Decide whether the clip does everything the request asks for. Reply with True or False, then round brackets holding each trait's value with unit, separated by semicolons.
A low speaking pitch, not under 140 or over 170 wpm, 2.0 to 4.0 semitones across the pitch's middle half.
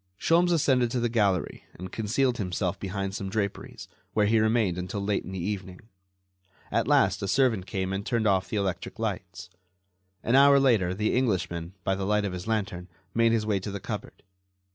False (100 Hz; 190 wpm; 3.4 semitones)